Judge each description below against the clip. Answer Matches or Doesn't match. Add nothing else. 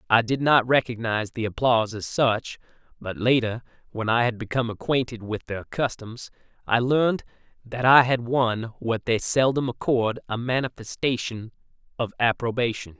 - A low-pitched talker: Matches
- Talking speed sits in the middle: Matches